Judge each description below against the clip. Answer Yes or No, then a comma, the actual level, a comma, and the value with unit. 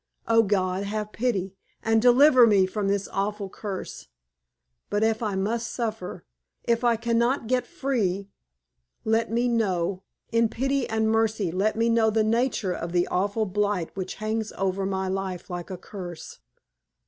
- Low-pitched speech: No, high, 215 Hz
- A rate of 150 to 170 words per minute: Yes, average, 160 wpm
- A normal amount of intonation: Yes, average, 3.1 semitones